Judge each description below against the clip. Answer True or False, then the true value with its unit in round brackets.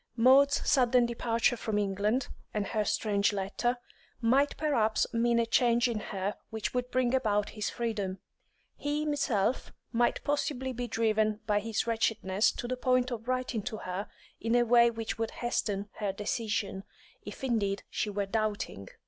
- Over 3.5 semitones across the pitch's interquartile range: False (2.9 semitones)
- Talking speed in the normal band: True (160 wpm)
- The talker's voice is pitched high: True (230 Hz)